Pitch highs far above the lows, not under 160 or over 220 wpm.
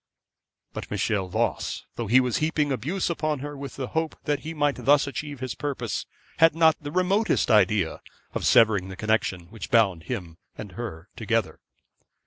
Yes: wide, 5.7 semitones; average, 170 wpm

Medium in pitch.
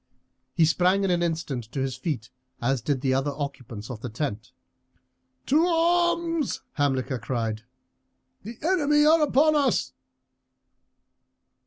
Yes: medium, 155 Hz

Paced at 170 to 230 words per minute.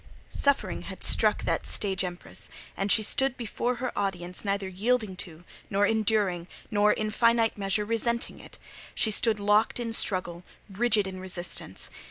No: average, 155 wpm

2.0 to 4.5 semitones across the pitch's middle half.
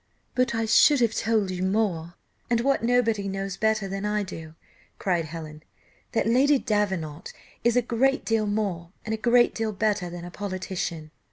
Yes: average, 3.9 semitones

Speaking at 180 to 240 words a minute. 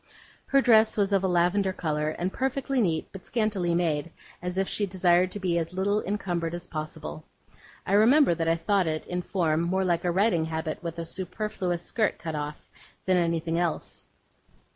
Yes: average, 185 wpm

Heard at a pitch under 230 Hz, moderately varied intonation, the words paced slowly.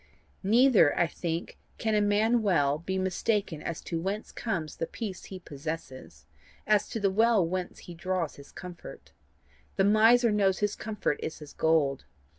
No: high, 190 Hz; average, 4.4 semitones; average, 165 wpm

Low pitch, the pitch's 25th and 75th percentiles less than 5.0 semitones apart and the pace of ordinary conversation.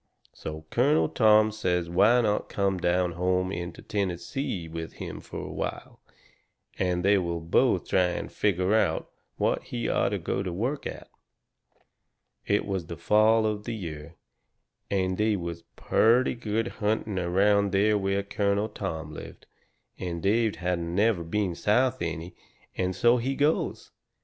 Yes: very low, 95 Hz; average, 3.6 semitones; average, 150 wpm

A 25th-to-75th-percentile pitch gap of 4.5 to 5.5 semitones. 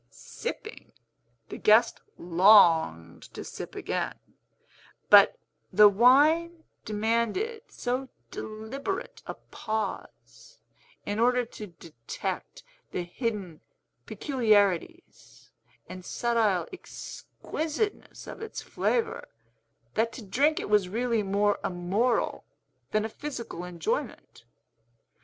Yes: average, 5.2 semitones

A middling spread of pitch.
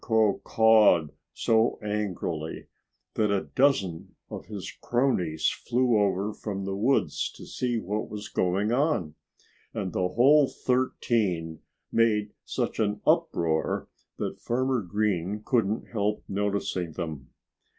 Yes: average, 3.9 semitones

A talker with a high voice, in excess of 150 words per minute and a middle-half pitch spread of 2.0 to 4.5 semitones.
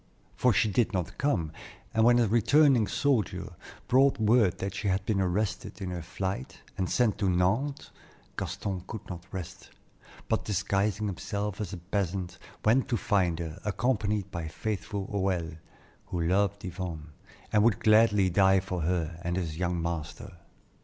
No: very low, 95 Hz; average, 160 wpm; average, 3.4 semitones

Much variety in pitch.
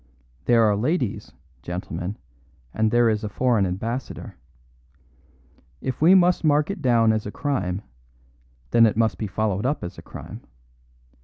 No: average, 4.2 semitones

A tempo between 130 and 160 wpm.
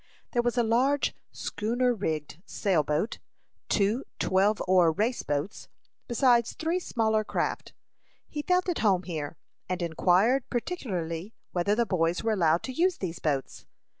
Yes: average, 145 wpm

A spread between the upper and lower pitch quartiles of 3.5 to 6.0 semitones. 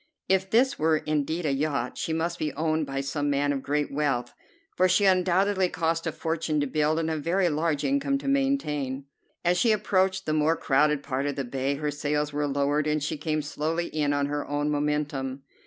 No: average, 2.8 semitones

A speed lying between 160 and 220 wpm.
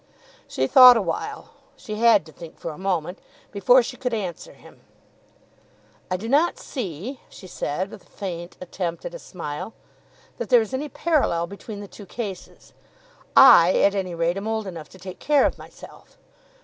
Yes: average, 175 wpm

